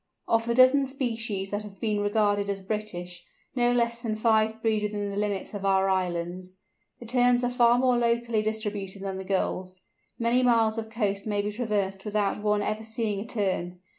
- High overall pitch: Yes, high, 210 Hz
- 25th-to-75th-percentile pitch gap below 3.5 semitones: Yes, average, 2.9 semitones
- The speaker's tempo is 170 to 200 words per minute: Yes, average, 190 wpm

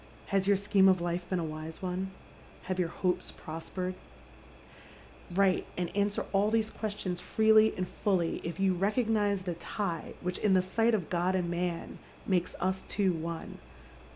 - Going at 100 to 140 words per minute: No, average, 170 wpm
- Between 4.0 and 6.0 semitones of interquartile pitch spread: No, narrow, 2.5 semitones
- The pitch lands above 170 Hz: Yes, medium, 185 Hz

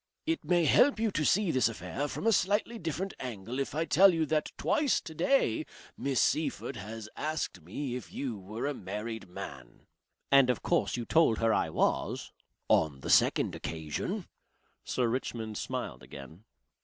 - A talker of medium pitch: No, low, 130 Hz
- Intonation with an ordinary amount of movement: No, wide, 7.3 semitones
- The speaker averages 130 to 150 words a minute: No, average, 170 wpm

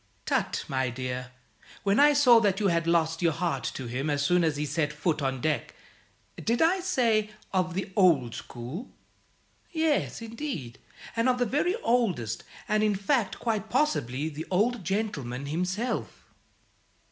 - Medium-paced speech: Yes, average, 160 wpm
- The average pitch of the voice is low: No, medium, 180 Hz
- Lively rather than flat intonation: Yes, wide, 7.9 semitones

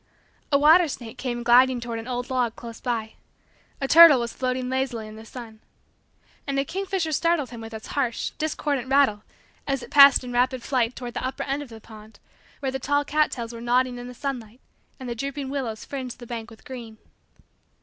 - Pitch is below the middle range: No, very high, 255 Hz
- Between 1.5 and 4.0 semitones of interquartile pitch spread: Yes, average, 2.8 semitones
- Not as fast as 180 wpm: No, fast, 205 wpm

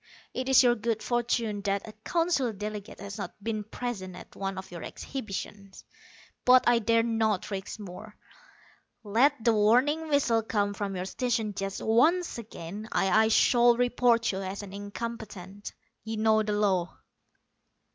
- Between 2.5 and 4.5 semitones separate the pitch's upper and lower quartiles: Yes, average, 3.1 semitones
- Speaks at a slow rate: No, average, 155 wpm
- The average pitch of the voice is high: Yes, high, 220 Hz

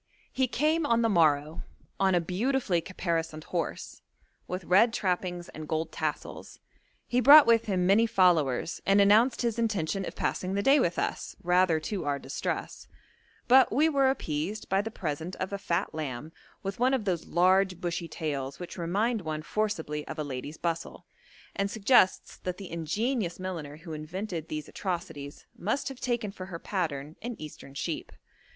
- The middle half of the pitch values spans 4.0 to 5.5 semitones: Yes, average, 5.2 semitones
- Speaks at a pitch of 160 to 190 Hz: Yes, medium, 185 Hz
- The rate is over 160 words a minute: Yes, average, 170 wpm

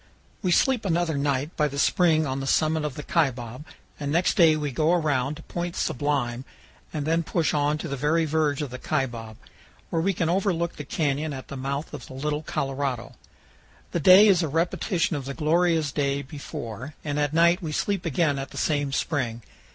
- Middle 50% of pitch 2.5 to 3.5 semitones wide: Yes, average, 3.2 semitones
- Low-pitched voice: No, medium, 150 Hz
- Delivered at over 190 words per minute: Yes, average, 200 wpm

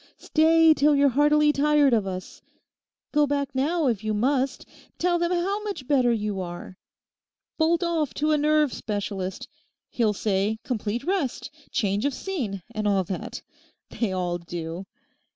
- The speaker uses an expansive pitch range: Yes, wide, 6.7 semitones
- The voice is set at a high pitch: Yes, very high, 265 Hz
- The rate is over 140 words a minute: Yes, average, 150 wpm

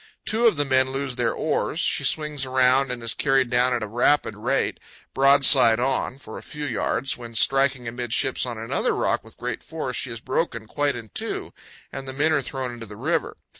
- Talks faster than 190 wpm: Yes, fast, 205 wpm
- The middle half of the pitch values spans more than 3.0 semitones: No, narrow, 2.4 semitones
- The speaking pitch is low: Yes, low, 130 Hz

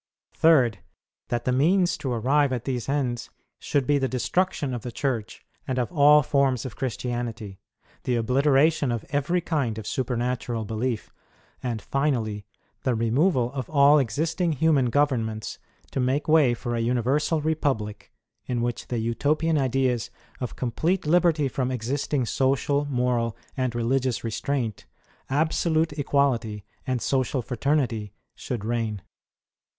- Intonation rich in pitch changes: No, average, 3.6 semitones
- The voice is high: No, low, 130 Hz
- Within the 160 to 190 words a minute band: No, slow, 135 wpm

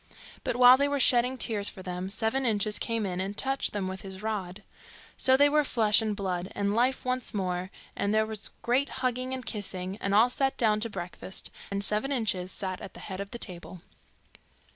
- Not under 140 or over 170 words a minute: No, fast, 205 wpm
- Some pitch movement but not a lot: Yes, average, 4.7 semitones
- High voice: Yes, high, 210 Hz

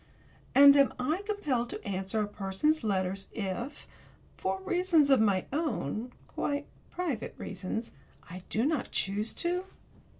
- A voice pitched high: Yes, high, 235 Hz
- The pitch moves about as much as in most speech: No, wide, 7.4 semitones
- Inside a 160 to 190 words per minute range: No, slow, 135 wpm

